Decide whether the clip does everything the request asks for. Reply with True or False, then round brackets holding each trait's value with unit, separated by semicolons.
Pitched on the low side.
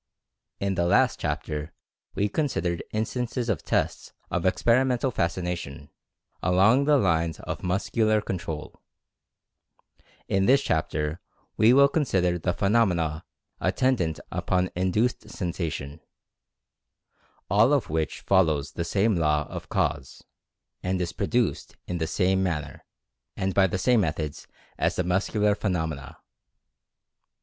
True (95 Hz)